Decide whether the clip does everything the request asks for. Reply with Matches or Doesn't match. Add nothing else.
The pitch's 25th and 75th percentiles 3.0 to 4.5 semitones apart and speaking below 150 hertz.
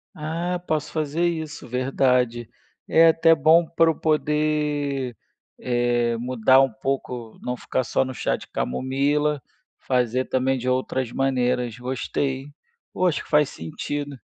Matches